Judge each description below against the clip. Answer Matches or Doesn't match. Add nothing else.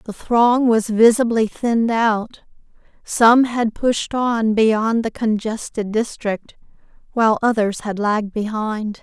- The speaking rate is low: Matches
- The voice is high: Matches